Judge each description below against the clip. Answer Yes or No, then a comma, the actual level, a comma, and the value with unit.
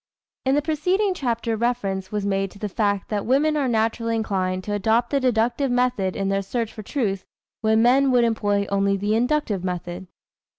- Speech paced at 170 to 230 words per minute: Yes, average, 195 wpm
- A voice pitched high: Yes, high, 220 Hz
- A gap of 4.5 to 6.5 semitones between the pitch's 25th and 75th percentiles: No, average, 4.0 semitones